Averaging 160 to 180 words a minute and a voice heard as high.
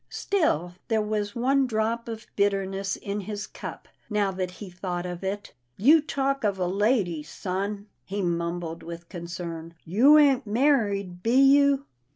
Yes: average, 165 wpm; high, 200 Hz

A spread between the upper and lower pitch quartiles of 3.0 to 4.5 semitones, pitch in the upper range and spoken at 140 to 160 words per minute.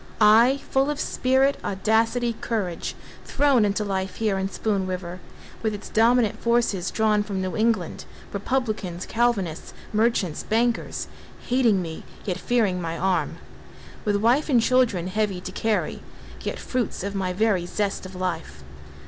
Yes: average, 3.9 semitones; high, 210 Hz; average, 145 wpm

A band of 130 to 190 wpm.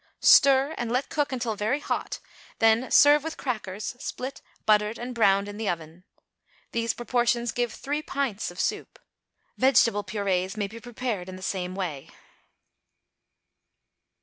Yes: average, 145 wpm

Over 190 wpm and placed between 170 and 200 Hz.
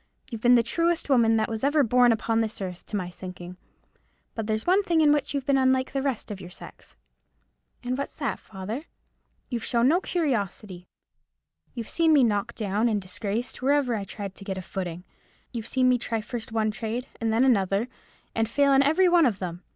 No: fast, 205 wpm; high, 230 Hz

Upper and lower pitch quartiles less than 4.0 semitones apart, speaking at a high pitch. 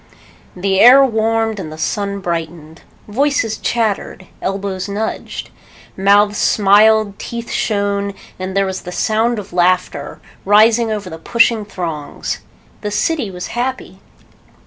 Yes: average, 2.9 semitones; high, 205 Hz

